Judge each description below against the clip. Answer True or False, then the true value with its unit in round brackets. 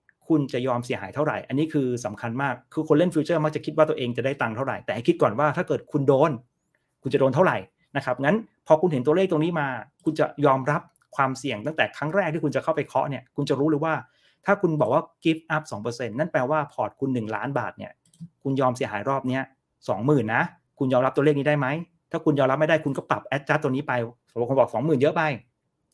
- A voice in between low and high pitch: True (145 Hz)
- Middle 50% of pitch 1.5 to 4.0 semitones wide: True (3.1 semitones)